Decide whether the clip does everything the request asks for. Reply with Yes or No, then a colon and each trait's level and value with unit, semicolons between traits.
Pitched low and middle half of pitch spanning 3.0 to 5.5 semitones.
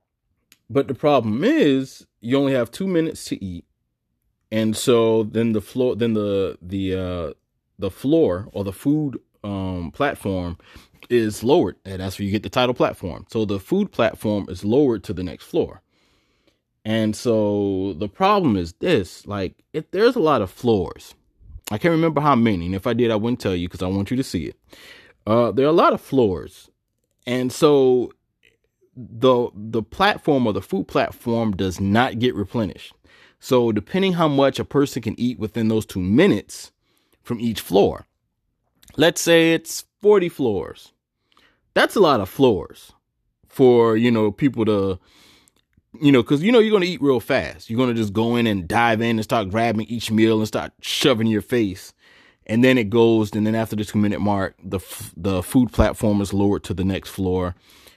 Yes: low, 110 Hz; average, 4.2 semitones